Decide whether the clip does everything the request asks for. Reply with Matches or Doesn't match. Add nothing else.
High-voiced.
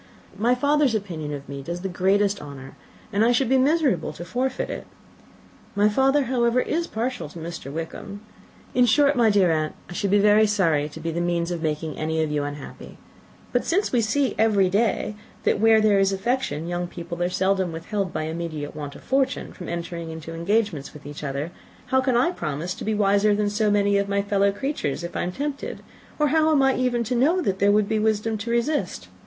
Matches